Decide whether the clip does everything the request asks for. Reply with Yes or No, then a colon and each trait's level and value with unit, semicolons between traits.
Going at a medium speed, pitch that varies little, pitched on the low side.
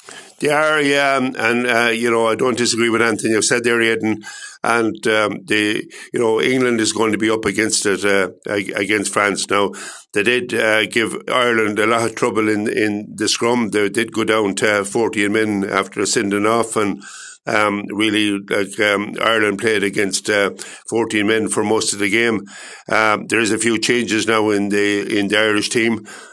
Yes: average, 195 wpm; narrow, 1.8 semitones; low, 110 Hz